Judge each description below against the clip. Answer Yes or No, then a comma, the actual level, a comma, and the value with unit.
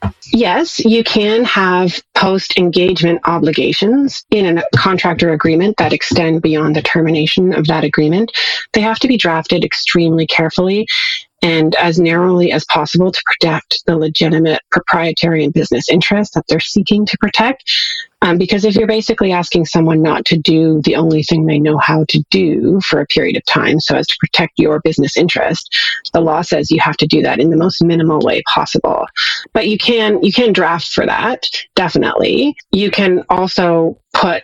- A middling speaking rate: Yes, average, 175 wpm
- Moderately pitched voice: Yes, medium, 175 Hz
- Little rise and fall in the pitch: No, average, 4.5 semitones